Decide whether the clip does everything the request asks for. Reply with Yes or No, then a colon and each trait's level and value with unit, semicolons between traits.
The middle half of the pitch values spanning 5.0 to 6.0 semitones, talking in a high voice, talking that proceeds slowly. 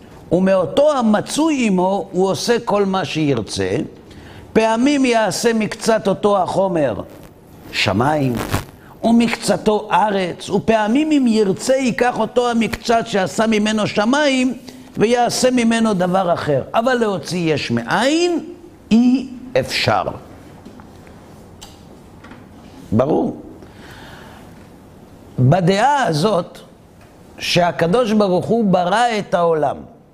Yes: wide, 5.5 semitones; high, 210 Hz; slow, 90 wpm